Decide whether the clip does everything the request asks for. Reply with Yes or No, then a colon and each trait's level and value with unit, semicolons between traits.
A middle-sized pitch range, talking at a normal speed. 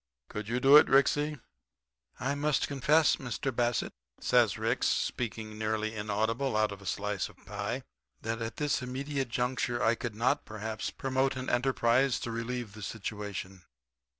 Yes: average, 3.7 semitones; average, 155 wpm